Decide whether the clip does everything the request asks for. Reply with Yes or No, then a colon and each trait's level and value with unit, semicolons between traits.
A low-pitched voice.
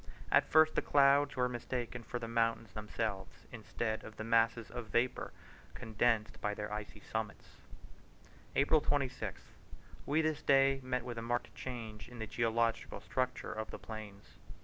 Yes: low, 115 Hz